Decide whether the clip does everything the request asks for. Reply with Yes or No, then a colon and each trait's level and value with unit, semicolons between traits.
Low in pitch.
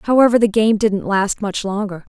No: high, 210 Hz